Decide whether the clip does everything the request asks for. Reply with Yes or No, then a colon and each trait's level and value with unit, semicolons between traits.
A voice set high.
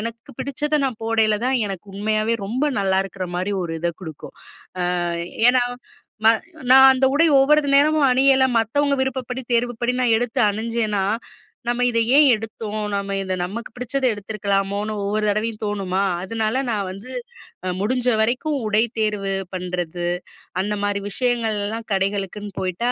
Yes: high, 220 Hz